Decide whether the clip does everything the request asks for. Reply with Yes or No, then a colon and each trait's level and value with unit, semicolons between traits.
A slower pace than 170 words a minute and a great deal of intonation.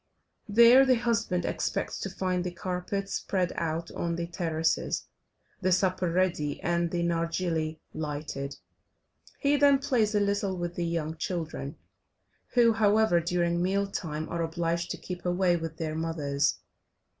No: average, 145 wpm; average, 3.2 semitones